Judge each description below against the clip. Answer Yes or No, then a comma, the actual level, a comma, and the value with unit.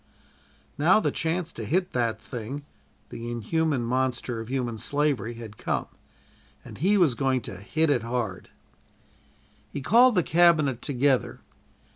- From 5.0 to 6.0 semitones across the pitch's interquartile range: Yes, average, 5.3 semitones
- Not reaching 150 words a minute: Yes, average, 140 wpm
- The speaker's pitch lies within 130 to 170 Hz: Yes, low, 135 Hz